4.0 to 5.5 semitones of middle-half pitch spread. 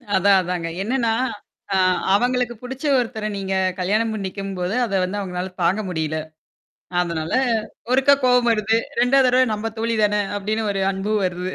Yes: average, 4.4 semitones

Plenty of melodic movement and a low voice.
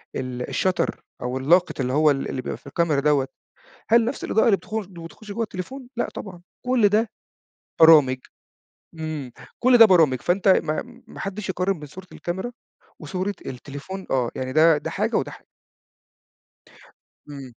No: wide, 6.2 semitones; medium, 170 Hz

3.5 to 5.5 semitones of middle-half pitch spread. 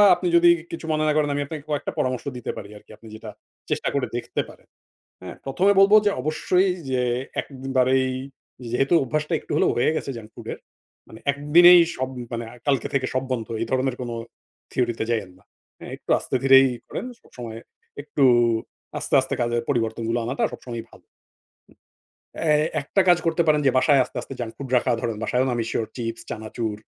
Yes: average, 4.1 semitones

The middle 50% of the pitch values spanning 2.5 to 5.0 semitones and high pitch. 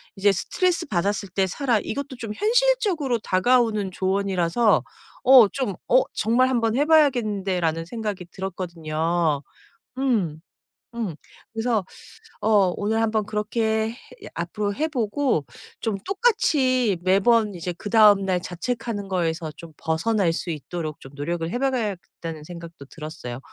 No: wide, 5.5 semitones; high, 205 Hz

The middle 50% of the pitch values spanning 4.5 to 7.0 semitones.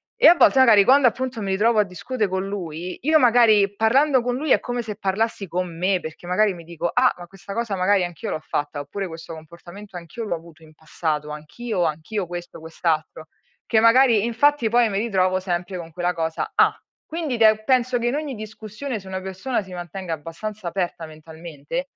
Yes: wide, 5.4 semitones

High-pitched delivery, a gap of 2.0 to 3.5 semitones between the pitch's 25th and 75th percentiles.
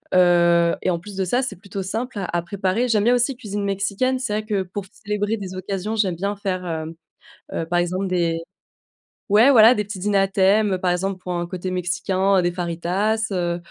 Yes: high, 195 Hz; average, 2.8 semitones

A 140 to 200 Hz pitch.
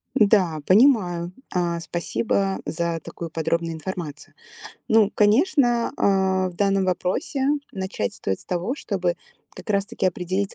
Yes: high, 190 Hz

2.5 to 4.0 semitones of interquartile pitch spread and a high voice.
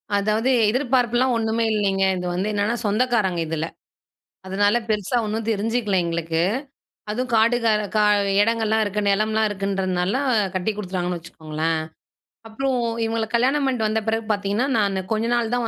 Yes: average, 3.0 semitones; high, 215 Hz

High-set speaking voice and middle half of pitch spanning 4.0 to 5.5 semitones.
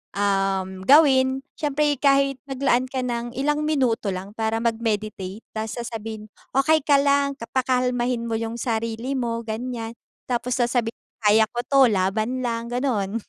No: high, 240 Hz; average, 3.2 semitones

